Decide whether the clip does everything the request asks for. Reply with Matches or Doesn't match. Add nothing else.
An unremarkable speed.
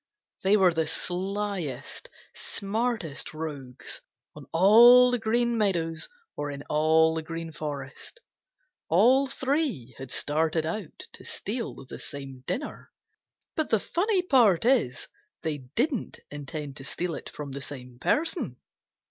Doesn't match